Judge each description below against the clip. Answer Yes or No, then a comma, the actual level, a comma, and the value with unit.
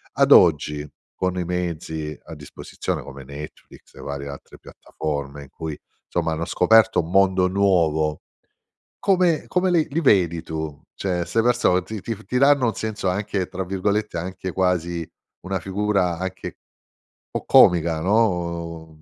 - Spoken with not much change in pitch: No, average, 3.9 semitones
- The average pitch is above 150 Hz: No, very low, 90 Hz